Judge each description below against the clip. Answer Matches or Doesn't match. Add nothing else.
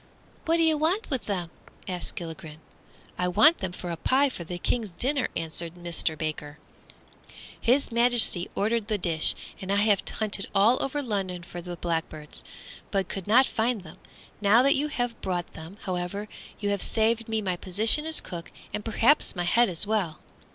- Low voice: Doesn't match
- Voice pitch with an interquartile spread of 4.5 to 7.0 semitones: Matches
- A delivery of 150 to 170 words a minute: Doesn't match